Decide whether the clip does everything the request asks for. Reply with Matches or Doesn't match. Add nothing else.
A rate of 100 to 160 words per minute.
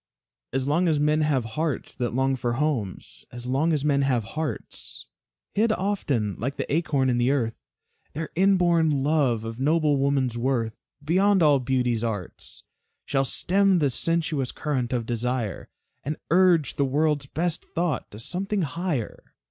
Matches